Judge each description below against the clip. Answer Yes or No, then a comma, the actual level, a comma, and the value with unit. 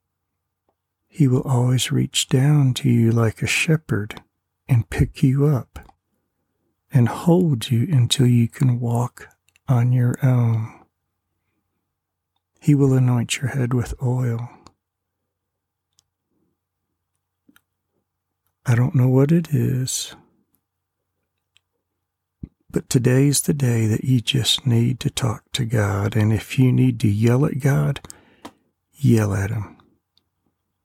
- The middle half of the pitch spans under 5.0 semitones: No, wide, 5.6 semitones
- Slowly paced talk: Yes, slow, 115 wpm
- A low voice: Yes, low, 115 Hz